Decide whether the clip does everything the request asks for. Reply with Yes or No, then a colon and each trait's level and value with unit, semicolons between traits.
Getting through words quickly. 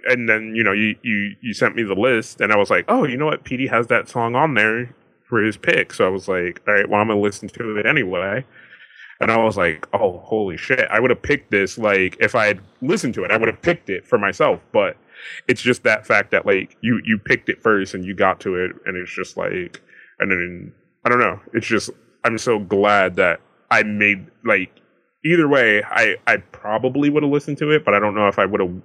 Yes: fast, 250 wpm